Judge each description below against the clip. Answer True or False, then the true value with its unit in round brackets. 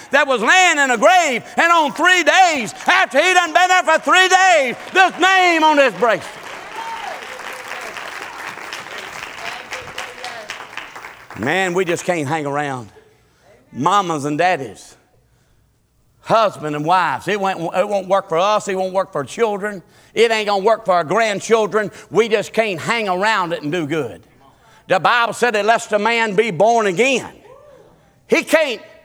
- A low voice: False (225 Hz)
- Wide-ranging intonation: True (8.8 semitones)